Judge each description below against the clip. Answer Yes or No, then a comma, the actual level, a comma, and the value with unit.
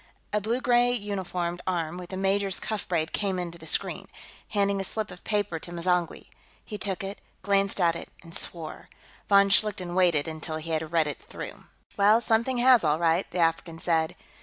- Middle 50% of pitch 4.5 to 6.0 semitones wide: No, average, 3.4 semitones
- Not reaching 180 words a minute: No, average, 190 wpm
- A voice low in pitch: No, medium, 185 Hz